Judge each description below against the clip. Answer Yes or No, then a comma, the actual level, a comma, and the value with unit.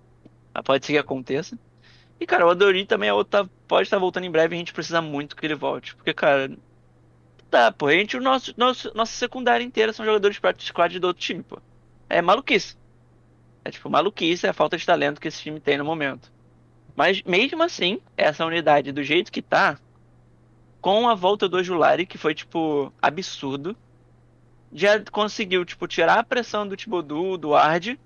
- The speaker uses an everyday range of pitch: No, wide, 6.3 semitones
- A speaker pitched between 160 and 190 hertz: Yes, medium, 175 Hz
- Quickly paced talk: Yes, fast, 190 wpm